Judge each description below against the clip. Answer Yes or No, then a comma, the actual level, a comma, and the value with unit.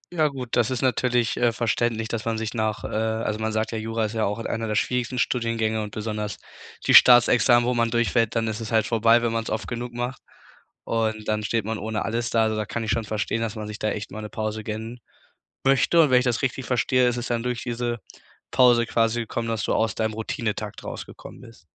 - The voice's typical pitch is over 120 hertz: No, low, 115 Hz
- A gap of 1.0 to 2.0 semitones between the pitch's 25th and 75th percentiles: Yes, narrow, 1.7 semitones